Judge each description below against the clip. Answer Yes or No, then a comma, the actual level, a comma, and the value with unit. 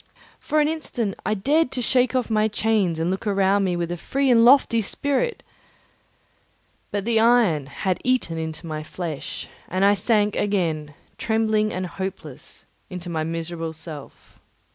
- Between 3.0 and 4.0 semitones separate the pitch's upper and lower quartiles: No, wide, 5.5 semitones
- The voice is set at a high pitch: Yes, high, 200 Hz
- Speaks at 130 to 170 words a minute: Yes, average, 160 wpm